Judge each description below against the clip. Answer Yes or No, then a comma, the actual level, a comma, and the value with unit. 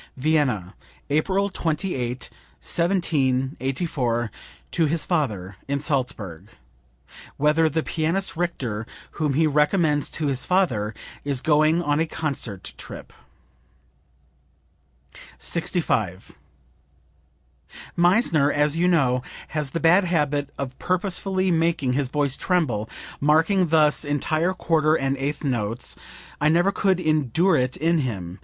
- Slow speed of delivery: Yes, slow, 115 wpm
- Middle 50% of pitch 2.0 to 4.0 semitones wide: No, average, 4.4 semitones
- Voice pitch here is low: No, medium, 150 Hz